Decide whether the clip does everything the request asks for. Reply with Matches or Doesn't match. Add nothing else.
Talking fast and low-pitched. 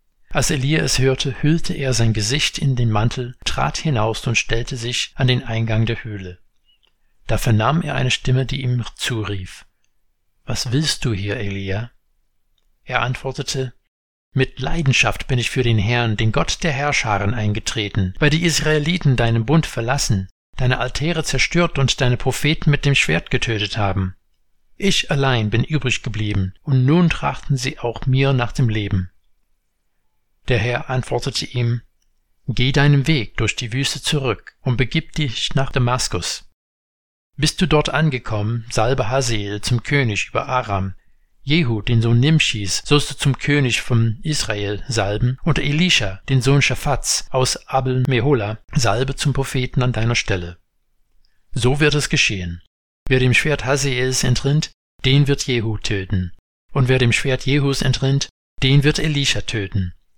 Doesn't match